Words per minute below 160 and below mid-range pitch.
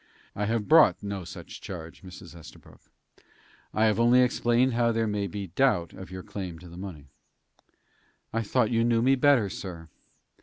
No: average, 175 wpm; low, 105 Hz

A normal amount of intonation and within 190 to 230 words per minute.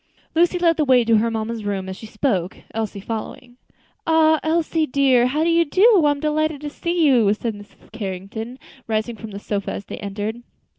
No: wide, 6.4 semitones; average, 195 wpm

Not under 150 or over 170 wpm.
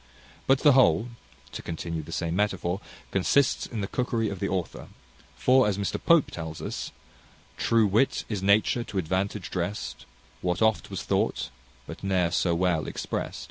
Yes: average, 165 wpm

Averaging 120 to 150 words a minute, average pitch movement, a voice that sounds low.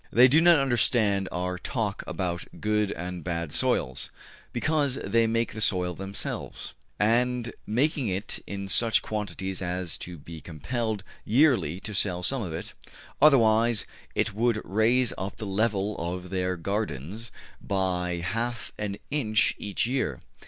Yes: average, 145 wpm; average, 4.3 semitones; low, 105 Hz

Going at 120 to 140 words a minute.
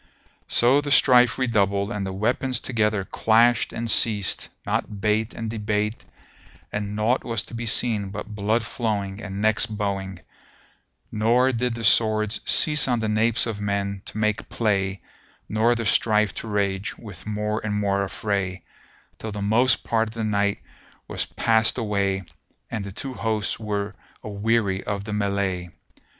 No: average, 160 wpm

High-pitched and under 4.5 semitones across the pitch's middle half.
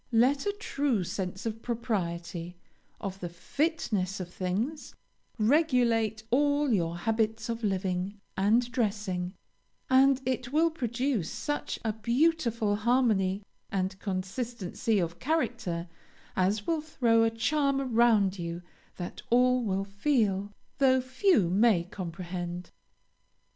No: high, 220 Hz; average, 5.2 semitones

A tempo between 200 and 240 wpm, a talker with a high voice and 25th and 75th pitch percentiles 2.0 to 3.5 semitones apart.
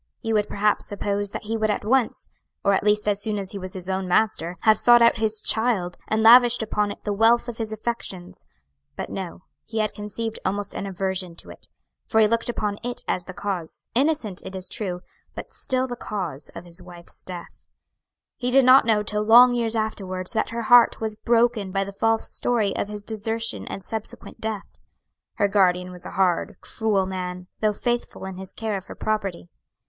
Yes: fast, 205 wpm; high, 210 Hz; average, 3.0 semitones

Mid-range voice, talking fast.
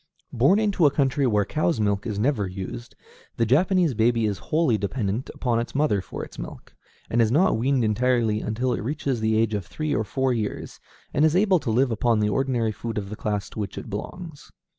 No: low, 120 Hz; fast, 210 wpm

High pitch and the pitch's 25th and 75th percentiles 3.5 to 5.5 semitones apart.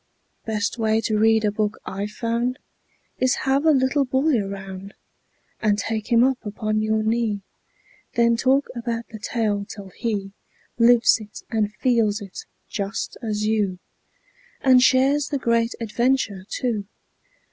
No: high, 225 Hz; average, 2.8 semitones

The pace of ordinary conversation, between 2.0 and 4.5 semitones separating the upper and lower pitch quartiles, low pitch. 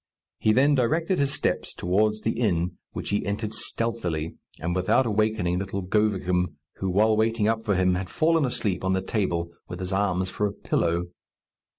Yes: average, 180 wpm; average, 3.7 semitones; low, 100 Hz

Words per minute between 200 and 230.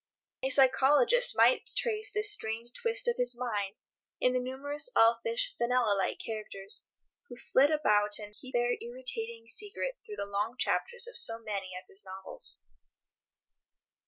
No: average, 150 wpm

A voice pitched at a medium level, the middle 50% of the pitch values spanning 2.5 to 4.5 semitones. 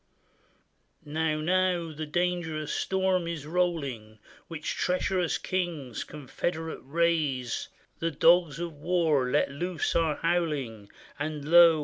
Yes: medium, 160 Hz; average, 2.9 semitones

